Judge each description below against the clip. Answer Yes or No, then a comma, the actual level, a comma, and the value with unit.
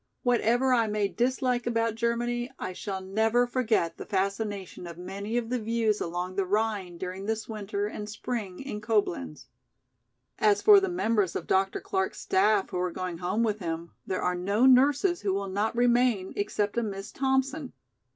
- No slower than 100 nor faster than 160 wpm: No, average, 175 wpm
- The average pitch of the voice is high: Yes, high, 210 Hz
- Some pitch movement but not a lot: Yes, average, 4.0 semitones